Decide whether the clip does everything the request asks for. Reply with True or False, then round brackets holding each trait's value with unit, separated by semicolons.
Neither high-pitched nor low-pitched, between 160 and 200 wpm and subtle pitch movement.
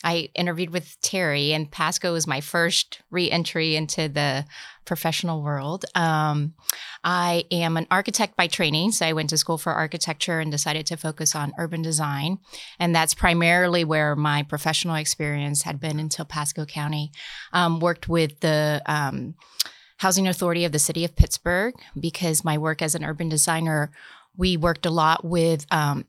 True (165 Hz; 170 wpm; 2.1 semitones)